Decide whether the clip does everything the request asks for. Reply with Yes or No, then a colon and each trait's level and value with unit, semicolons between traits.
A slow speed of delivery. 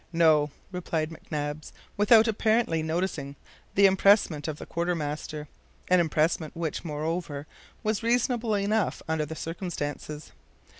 Yes: slow, 115 wpm